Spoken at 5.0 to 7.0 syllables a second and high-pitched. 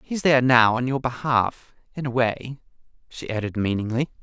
No: 5.4 syllables/s; low, 125 Hz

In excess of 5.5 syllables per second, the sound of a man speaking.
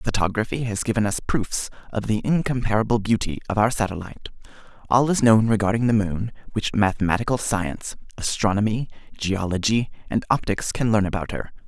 Yes: 5.7 syllables/s; male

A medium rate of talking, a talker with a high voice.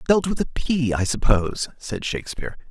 No: average, 180 wpm; low, 130 Hz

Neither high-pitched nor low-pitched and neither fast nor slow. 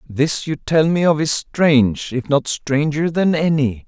Yes: medium, 145 Hz; average, 170 wpm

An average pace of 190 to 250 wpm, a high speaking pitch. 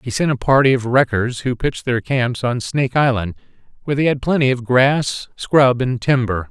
No: fast, 205 wpm; low, 125 Hz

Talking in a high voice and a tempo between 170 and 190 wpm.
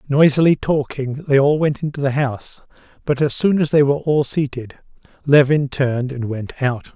No: medium, 140 Hz; average, 180 wpm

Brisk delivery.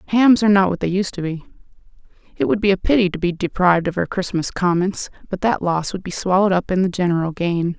Yes: fast, 240 wpm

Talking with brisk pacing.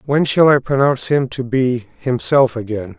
No: average, 180 wpm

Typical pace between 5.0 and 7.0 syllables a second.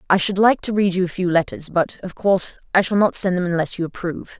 Yes: 6.2 syllables/s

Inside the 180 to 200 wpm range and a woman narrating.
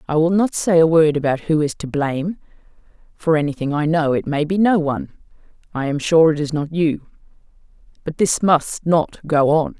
Yes: average, 190 wpm; female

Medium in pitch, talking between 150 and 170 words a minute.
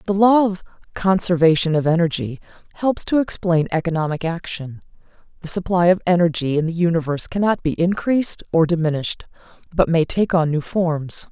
Yes: medium, 170 Hz; average, 155 wpm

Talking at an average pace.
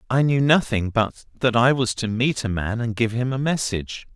No: fast, 230 wpm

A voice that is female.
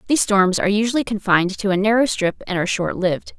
Yes: female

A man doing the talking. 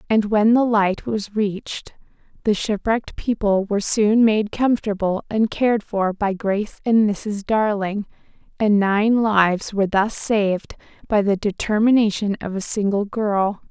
No: female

